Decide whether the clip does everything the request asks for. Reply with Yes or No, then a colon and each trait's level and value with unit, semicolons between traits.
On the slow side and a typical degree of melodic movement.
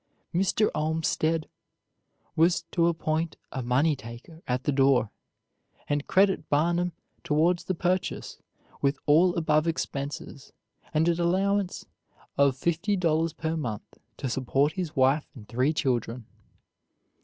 Yes: slow, 125 wpm; average, 3.8 semitones